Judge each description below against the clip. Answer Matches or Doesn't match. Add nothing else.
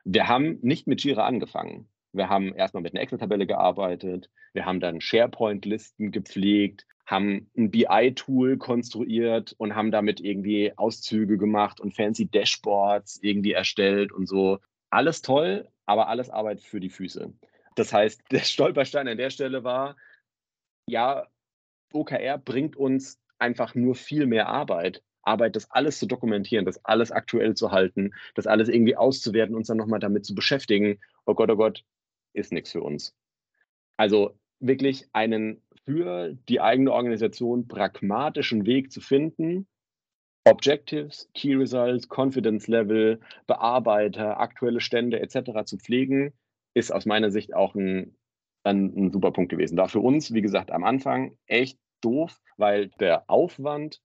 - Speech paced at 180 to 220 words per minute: Doesn't match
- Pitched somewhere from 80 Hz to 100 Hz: Doesn't match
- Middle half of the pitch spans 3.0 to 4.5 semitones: Matches